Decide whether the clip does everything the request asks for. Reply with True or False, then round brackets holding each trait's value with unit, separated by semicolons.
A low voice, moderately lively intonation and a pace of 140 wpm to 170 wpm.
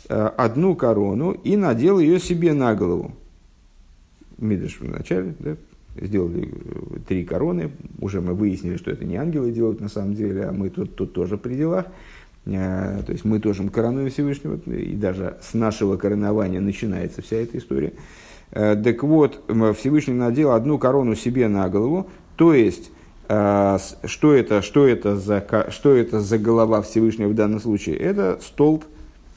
True (110 Hz; 4.2 semitones; 150 wpm)